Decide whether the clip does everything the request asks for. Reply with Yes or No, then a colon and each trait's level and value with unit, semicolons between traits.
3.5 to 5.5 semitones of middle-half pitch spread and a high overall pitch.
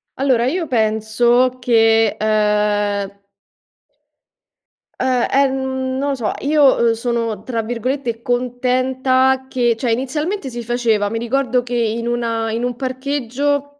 No: narrow, 2.5 semitones; high, 245 Hz